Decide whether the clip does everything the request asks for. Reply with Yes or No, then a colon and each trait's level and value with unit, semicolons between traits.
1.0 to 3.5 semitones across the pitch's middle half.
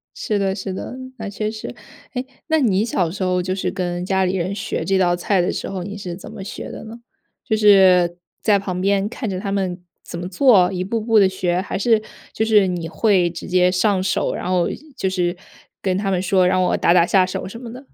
Yes: narrow, 2.4 semitones